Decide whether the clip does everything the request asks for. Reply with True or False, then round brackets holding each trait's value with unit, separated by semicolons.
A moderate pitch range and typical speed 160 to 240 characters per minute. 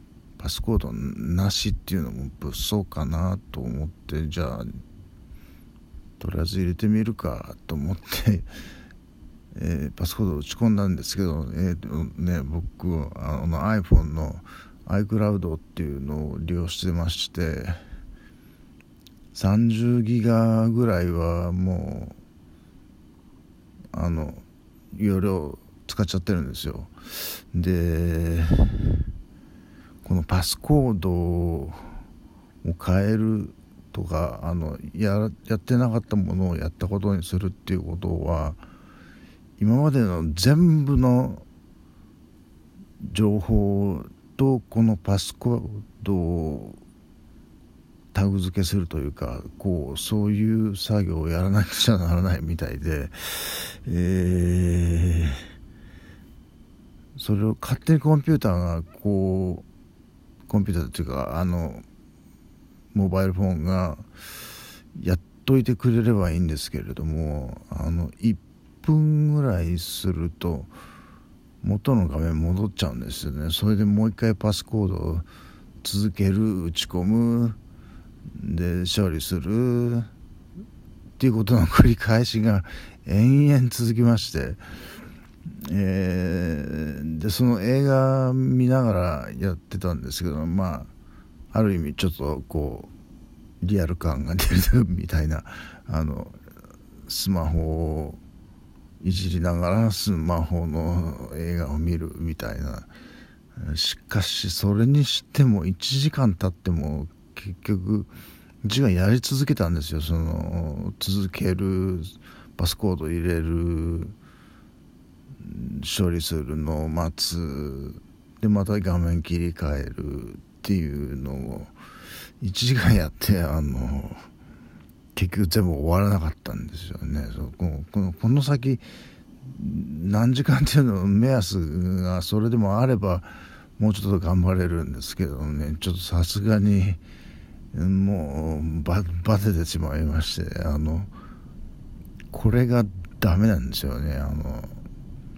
True (4.4 semitones; 230 characters per minute)